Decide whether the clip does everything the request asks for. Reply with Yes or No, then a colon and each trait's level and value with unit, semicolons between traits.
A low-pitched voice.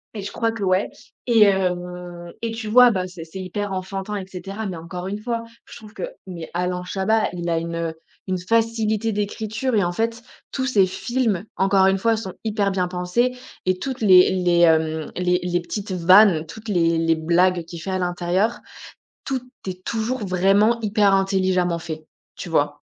No: high, 190 Hz